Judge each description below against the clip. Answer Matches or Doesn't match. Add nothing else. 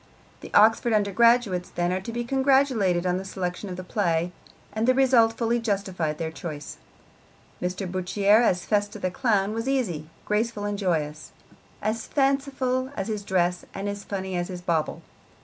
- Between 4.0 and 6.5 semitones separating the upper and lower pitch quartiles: Matches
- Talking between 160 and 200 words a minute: Matches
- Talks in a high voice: Matches